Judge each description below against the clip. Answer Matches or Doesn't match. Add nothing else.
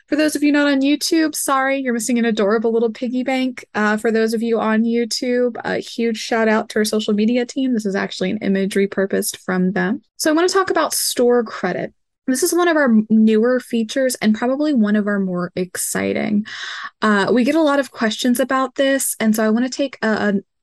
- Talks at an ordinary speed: Doesn't match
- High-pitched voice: Matches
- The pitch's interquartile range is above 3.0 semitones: Matches